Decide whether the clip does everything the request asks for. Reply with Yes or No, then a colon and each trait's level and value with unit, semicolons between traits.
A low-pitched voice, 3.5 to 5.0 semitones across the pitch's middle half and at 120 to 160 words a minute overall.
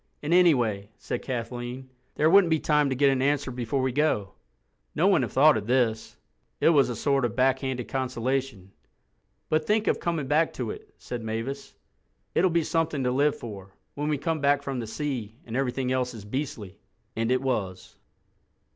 No: low, 130 Hz; average, 3.9 semitones; average, 185 wpm